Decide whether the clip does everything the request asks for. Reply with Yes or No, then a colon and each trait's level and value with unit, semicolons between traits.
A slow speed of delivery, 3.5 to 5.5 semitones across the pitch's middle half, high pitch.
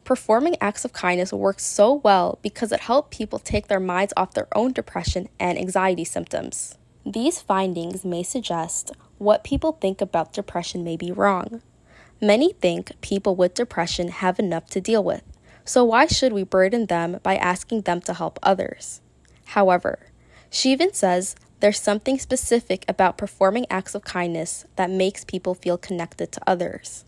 No: average, 165 wpm; average, 4.3 semitones; high, 195 Hz